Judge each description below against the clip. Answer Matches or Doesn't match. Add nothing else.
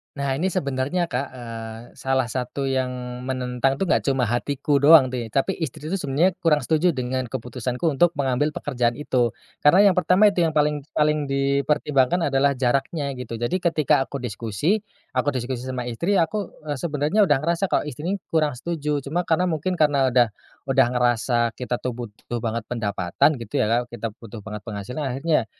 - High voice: Doesn't match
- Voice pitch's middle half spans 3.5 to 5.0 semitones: Matches